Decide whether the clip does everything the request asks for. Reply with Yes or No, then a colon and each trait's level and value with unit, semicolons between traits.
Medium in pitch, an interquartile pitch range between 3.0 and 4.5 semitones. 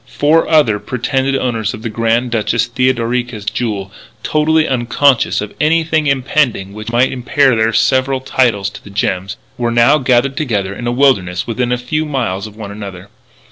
No: low, 120 Hz; average, 3.9 semitones